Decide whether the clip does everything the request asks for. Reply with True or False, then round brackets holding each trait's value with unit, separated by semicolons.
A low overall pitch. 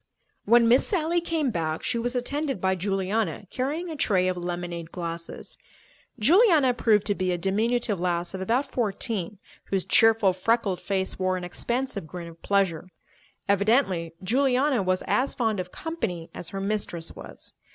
False (200 Hz)